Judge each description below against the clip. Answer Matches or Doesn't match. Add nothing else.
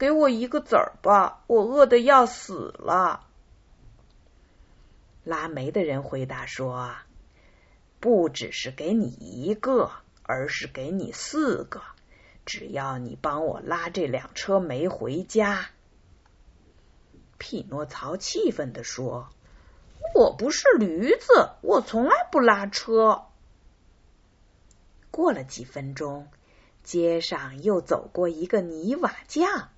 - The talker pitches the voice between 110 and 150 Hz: Doesn't match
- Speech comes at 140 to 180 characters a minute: Matches